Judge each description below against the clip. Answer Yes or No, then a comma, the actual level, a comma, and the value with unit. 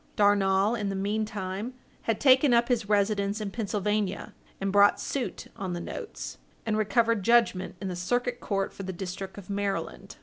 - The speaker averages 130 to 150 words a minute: No, average, 170 wpm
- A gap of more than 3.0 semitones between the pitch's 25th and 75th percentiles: No, average, 2.7 semitones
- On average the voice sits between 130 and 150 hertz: No, high, 205 Hz